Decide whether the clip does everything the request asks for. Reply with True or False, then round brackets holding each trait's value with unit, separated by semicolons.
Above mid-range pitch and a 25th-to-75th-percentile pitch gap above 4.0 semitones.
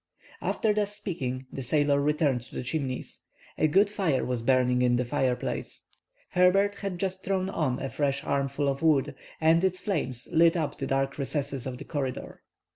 False (145 Hz; 5.6 semitones)